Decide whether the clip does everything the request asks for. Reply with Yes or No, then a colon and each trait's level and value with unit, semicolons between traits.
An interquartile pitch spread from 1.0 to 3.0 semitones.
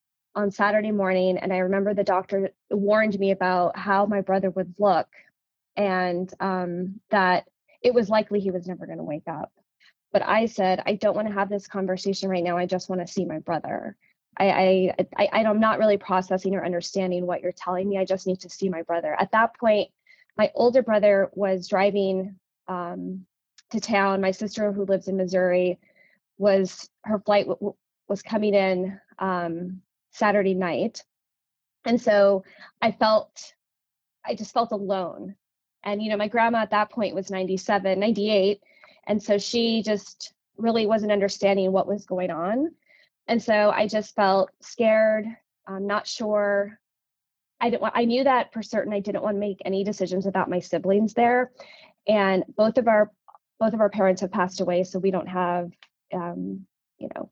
Yes: narrow, 2.4 semitones